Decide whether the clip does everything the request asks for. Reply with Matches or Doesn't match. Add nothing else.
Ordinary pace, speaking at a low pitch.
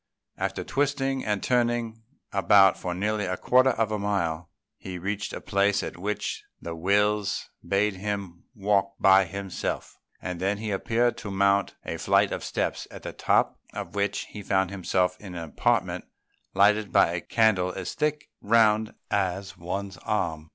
Matches